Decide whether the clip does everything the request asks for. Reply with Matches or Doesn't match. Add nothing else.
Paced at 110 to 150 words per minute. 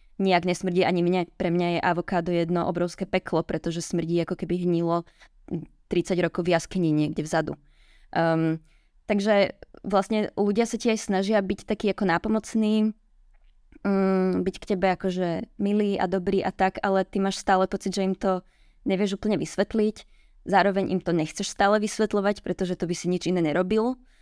Doesn't match